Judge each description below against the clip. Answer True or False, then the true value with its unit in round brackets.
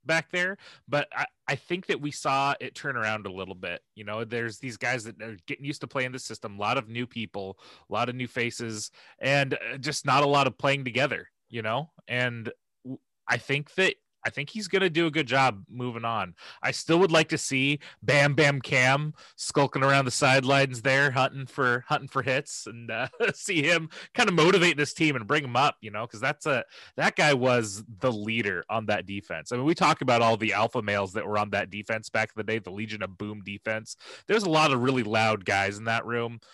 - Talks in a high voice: False (130 Hz)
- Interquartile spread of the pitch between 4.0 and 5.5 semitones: True (4.5 semitones)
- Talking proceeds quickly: True (230 wpm)